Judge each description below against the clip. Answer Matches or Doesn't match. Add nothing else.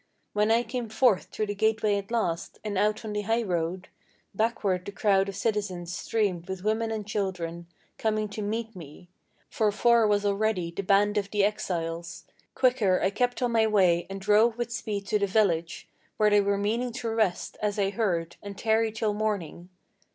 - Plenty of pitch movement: Doesn't match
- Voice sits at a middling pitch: Doesn't match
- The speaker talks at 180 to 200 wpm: Matches